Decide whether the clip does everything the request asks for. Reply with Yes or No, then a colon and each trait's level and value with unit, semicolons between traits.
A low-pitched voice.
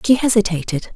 No: high, 205 Hz